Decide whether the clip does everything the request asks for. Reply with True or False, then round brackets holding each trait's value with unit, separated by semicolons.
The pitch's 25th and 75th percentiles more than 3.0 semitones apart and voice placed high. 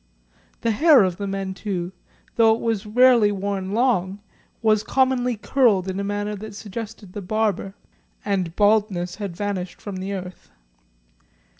False (2.7 semitones; 205 Hz)